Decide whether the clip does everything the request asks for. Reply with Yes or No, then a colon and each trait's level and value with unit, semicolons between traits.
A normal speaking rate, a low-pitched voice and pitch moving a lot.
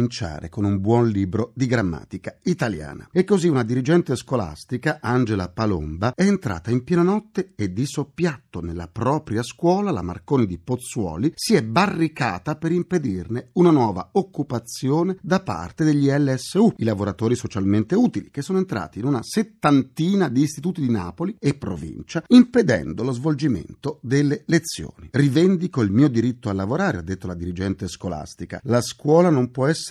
Yes: average, 155 wpm; low, 130 Hz; wide, 7.5 semitones